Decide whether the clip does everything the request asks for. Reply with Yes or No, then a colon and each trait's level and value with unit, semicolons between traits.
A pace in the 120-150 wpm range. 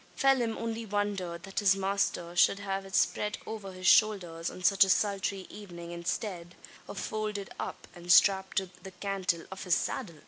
No: average, 175 wpm